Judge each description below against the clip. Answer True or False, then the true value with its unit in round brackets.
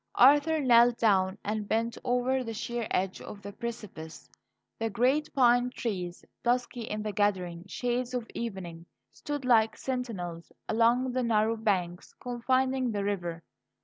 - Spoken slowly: False (145 wpm)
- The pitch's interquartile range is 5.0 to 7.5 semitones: False (3.8 semitones)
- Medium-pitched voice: False (230 Hz)